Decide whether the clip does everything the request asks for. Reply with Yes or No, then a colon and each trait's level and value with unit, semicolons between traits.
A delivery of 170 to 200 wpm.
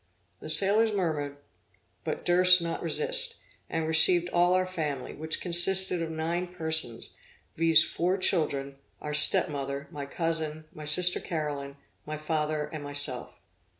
No: average, 140 wpm